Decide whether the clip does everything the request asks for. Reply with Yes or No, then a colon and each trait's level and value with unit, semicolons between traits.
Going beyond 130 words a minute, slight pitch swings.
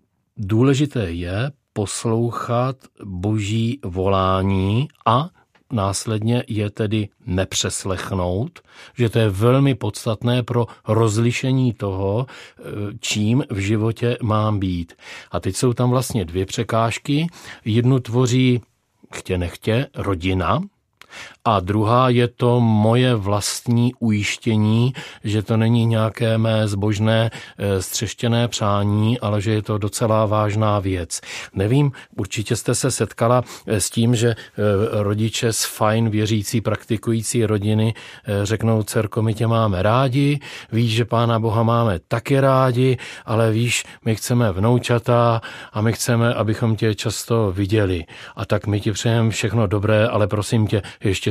No: average, 125 wpm; narrow, 2.3 semitones